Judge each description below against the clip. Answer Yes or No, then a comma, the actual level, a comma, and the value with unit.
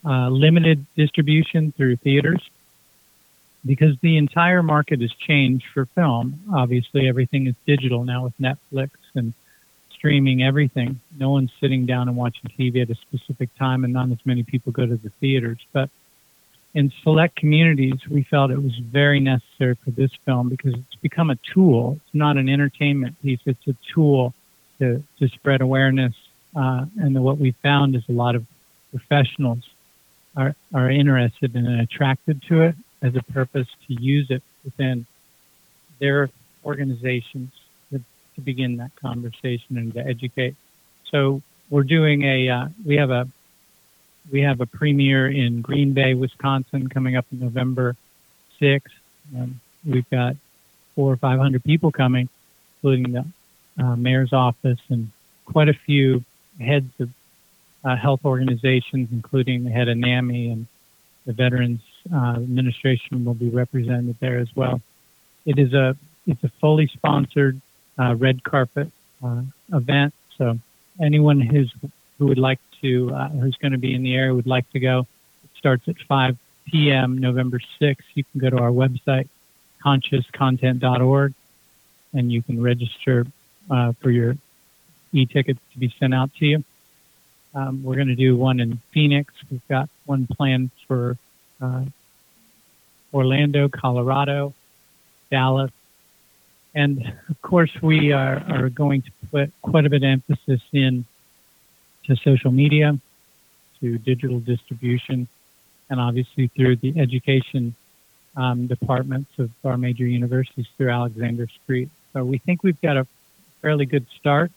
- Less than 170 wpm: Yes, average, 150 wpm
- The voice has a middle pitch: No, low, 130 Hz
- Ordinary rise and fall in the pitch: No, narrow, 2.2 semitones